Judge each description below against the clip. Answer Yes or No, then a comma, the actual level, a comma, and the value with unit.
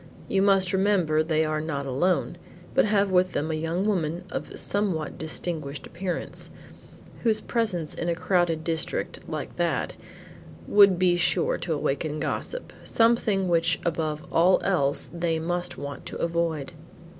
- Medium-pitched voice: Yes, medium, 170 Hz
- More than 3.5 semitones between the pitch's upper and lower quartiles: No, average, 3.2 semitones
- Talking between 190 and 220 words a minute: No, average, 150 wpm